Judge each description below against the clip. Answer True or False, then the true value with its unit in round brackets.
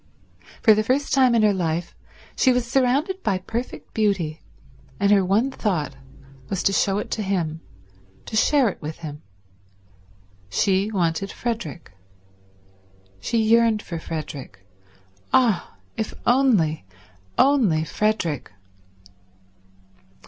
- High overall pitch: True (205 Hz)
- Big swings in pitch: True (6.1 semitones)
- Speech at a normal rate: False (120 wpm)